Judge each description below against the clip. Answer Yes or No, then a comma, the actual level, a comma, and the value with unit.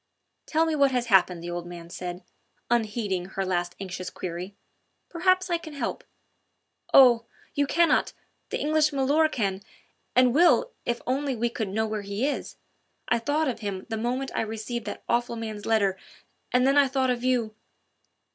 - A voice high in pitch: Yes, high, 235 Hz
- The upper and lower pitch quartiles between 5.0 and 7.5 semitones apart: Yes, wide, 5.6 semitones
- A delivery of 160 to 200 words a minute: Yes, average, 175 wpm